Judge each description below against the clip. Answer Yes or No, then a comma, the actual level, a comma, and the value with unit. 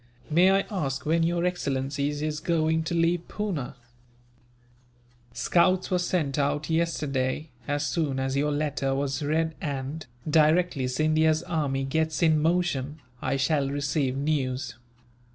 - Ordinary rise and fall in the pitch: Yes, average, 3.1 semitones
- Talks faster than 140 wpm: No, slow, 135 wpm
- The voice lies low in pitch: No, medium, 150 Hz